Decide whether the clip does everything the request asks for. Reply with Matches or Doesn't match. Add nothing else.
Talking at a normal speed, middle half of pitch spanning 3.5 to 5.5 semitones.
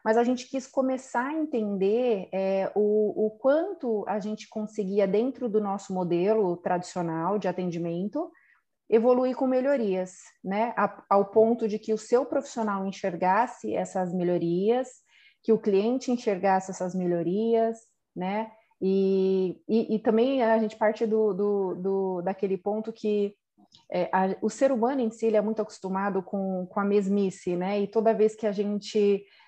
Doesn't match